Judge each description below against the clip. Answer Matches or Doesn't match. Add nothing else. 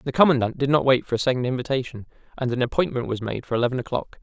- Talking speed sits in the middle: Doesn't match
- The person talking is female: Doesn't match